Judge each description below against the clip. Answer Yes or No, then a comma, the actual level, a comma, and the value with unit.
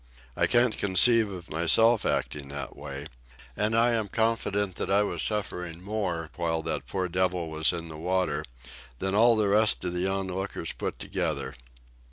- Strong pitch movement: No, average, 4.1 semitones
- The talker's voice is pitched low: Yes, very low, 95 Hz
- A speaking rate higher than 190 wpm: No, average, 170 wpm